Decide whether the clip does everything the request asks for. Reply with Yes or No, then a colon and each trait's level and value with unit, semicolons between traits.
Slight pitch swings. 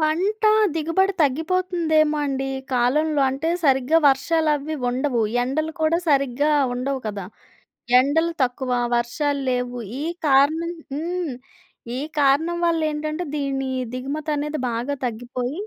No: average, 3.3 semitones